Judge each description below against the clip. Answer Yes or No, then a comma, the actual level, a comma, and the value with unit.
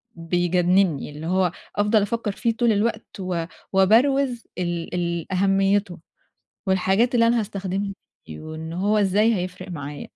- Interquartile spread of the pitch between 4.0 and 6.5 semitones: No, average, 3.3 semitones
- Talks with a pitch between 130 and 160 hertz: No, high, 190 Hz